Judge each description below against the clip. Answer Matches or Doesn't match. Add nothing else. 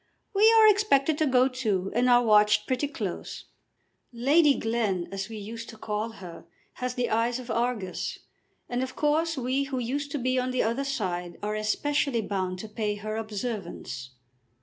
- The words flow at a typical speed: Matches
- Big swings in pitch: Doesn't match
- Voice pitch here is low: Doesn't match